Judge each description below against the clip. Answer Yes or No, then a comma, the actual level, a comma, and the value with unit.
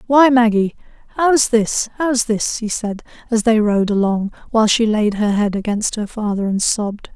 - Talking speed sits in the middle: Yes, average, 185 wpm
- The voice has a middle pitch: No, high, 220 Hz